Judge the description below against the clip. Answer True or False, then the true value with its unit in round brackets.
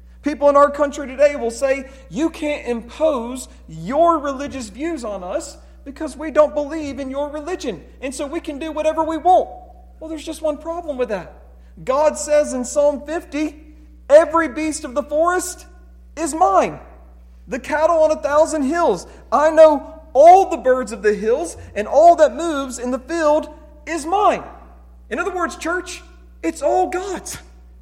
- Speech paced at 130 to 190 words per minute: True (170 wpm)